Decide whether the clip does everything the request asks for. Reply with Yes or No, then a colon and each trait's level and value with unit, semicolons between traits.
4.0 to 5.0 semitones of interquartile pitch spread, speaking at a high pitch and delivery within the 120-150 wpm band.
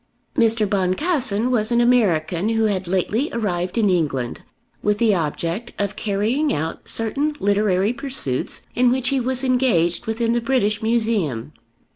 Yes: average, 4.7 semitones; high, 215 Hz; average, 145 wpm